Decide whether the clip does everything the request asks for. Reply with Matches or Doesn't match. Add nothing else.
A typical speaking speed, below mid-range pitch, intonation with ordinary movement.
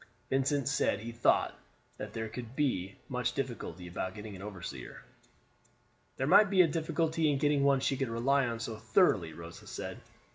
Matches